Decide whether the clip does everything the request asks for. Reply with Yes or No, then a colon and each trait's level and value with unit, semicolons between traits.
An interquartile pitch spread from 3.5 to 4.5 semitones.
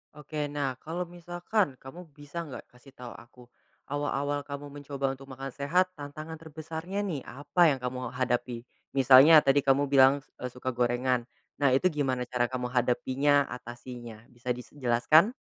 No: average, 3.0 semitones